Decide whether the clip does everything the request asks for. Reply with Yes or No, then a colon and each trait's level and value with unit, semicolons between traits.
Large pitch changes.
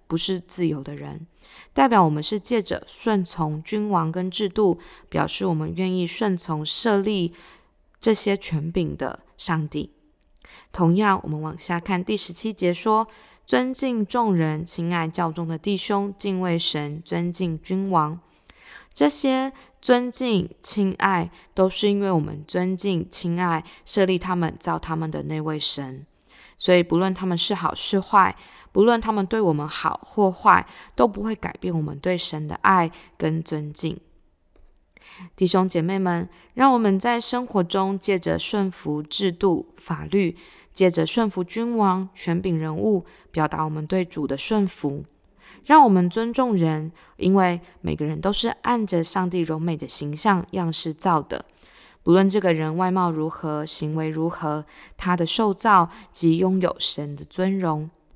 No: average, 3.7 semitones